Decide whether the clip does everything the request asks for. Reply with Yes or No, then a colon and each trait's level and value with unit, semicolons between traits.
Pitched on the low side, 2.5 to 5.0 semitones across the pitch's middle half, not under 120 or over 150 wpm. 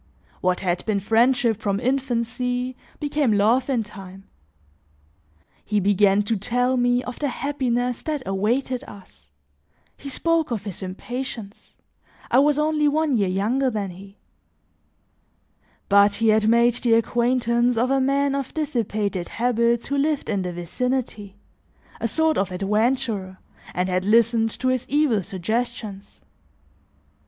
No: high, 235 Hz; average, 4.3 semitones; slow, 135 wpm